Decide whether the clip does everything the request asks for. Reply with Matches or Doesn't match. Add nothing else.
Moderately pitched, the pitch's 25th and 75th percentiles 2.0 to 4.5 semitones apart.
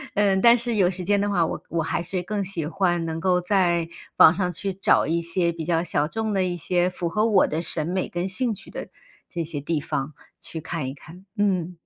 Matches